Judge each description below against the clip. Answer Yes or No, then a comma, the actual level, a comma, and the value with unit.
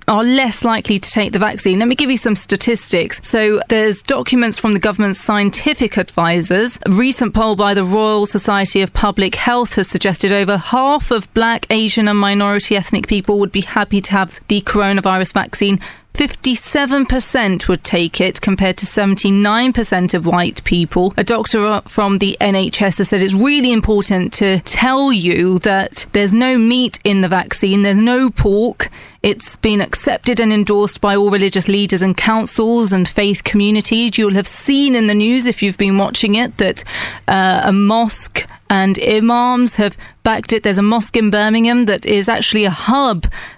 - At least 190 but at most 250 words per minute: No, average, 175 wpm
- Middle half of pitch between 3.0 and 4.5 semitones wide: No, narrow, 2.6 semitones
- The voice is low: No, high, 210 Hz